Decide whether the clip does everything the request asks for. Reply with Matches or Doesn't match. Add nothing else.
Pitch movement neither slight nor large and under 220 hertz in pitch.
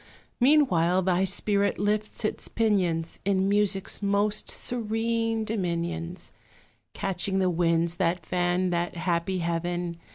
Matches